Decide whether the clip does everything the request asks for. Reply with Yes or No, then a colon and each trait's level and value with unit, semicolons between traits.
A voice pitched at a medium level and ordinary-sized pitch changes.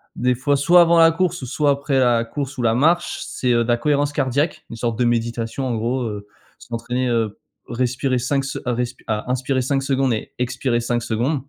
No: low, 125 Hz; average, 3.0 semitones